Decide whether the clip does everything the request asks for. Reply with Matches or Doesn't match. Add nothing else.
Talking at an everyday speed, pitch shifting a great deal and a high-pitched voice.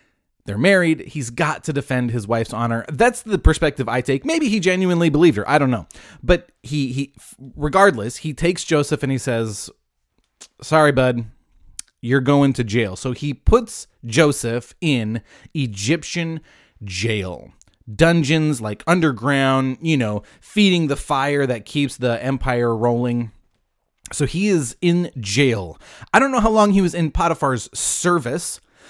Doesn't match